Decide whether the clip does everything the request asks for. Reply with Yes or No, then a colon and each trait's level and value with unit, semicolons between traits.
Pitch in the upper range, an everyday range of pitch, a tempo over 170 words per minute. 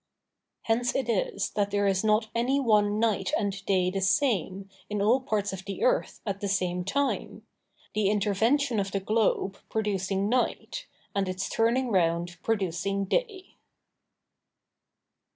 No: high, 205 Hz; average, 3.0 semitones; average, 145 wpm